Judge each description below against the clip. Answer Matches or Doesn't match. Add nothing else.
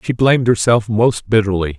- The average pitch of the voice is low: Matches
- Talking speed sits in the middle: Matches